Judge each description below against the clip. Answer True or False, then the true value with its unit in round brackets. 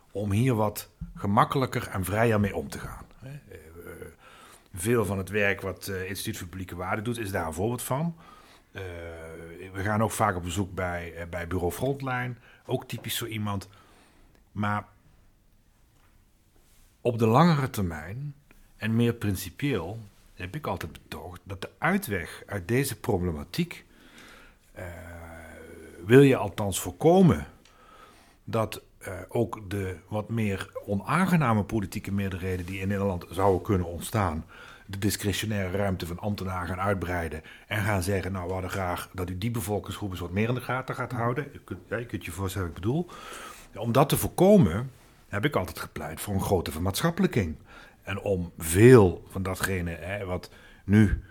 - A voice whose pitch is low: True (100 Hz)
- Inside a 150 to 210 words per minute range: True (155 wpm)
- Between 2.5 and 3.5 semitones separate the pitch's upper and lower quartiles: False (3.9 semitones)